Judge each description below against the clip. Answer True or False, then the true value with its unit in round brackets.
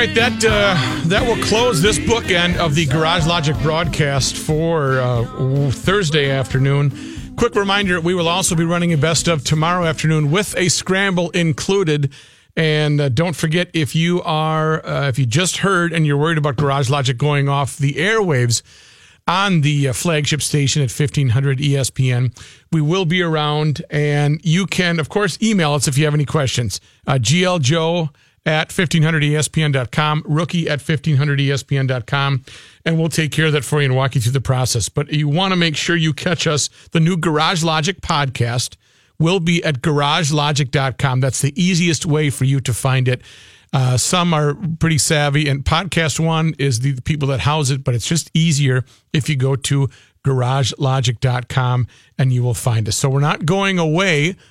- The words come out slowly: False (175 wpm)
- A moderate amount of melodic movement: True (3.5 semitones)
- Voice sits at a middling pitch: True (150 Hz)